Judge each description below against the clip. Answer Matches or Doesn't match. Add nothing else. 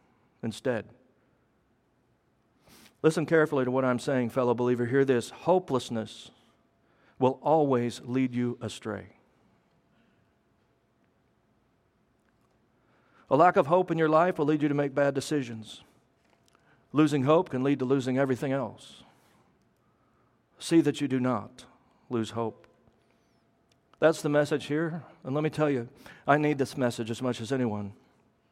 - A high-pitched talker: Doesn't match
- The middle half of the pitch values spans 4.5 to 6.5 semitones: Doesn't match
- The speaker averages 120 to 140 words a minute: Matches